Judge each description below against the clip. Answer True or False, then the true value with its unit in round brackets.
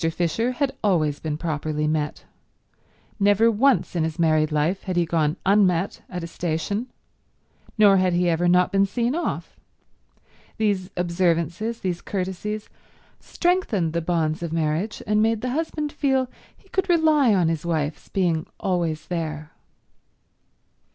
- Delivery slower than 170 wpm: True (145 wpm)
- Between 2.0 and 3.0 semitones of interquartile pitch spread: False (4.9 semitones)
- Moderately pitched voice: True (180 Hz)